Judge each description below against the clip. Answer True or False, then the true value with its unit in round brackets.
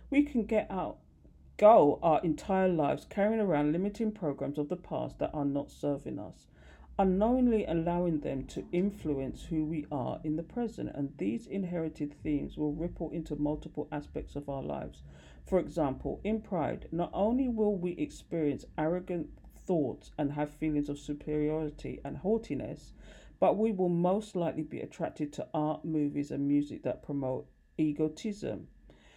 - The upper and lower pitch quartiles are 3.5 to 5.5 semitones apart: True (4.0 semitones)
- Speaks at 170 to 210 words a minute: False (155 wpm)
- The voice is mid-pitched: True (155 Hz)